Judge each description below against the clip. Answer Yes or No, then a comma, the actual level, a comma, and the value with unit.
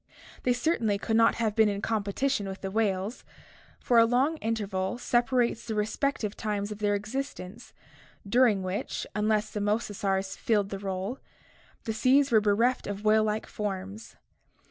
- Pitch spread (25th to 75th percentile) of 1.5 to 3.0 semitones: Yes, average, 2.7 semitones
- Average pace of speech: Yes, average, 155 wpm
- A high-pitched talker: Yes, high, 215 Hz